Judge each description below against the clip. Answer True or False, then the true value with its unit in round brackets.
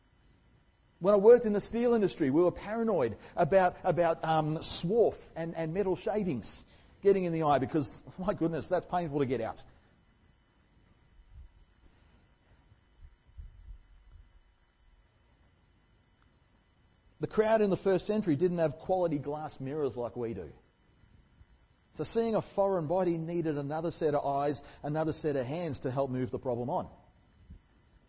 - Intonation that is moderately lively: False (8.9 semitones)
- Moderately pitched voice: True (150 Hz)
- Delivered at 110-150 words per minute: True (140 wpm)